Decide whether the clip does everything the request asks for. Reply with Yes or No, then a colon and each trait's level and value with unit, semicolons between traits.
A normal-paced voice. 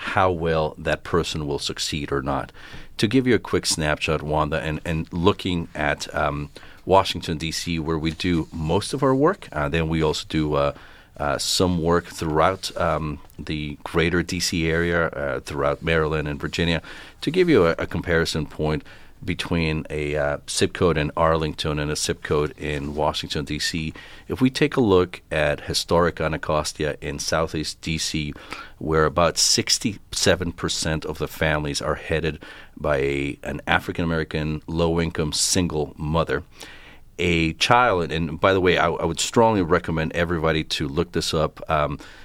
Yes: average, 165 wpm